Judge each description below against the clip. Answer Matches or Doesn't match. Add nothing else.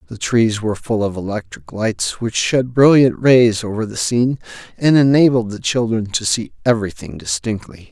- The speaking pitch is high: Doesn't match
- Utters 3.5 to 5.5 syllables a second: Matches